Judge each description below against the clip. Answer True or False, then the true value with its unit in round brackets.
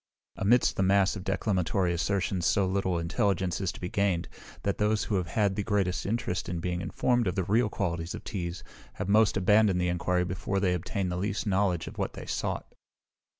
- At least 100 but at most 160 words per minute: False (200 wpm)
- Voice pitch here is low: True (95 Hz)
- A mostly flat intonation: True (2.2 semitones)